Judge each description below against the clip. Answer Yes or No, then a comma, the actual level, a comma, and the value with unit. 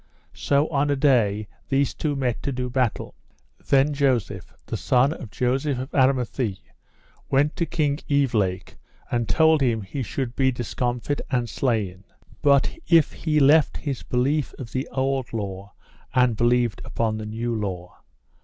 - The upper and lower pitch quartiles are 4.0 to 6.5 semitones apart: No, average, 3.4 semitones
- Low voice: Yes, low, 130 Hz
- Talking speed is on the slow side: No, average, 155 wpm